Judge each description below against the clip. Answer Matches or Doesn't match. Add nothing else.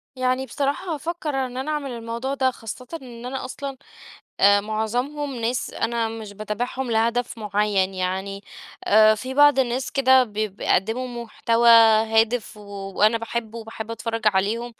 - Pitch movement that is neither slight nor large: Matches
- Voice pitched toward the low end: Doesn't match